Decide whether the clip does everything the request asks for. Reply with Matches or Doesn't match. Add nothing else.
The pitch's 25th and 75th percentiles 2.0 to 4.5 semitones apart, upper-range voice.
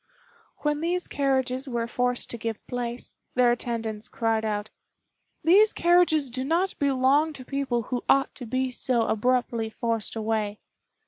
Matches